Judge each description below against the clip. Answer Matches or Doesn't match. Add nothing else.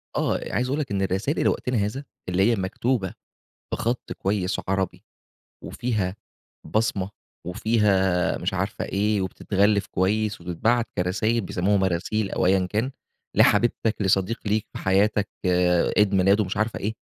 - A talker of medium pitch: Doesn't match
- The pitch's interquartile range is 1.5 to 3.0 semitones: Matches